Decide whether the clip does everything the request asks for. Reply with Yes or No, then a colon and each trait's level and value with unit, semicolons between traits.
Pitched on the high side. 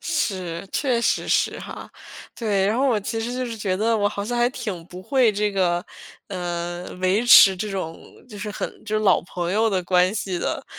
Yes: high, 205 Hz